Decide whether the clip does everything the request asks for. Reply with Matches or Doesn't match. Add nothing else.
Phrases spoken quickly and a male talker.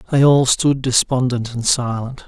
Doesn't match